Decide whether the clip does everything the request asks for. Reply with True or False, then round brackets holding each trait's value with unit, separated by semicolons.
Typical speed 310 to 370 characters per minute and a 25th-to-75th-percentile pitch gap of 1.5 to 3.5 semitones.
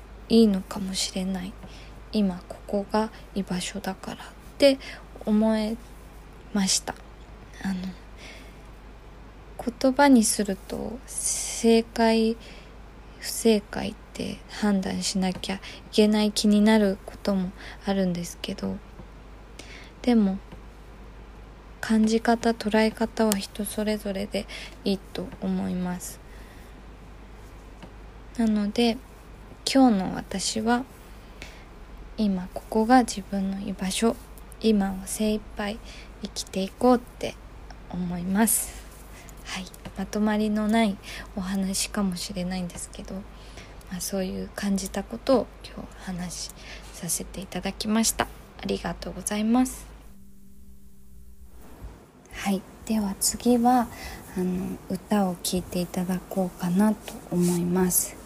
False (215 characters per minute; 2.9 semitones)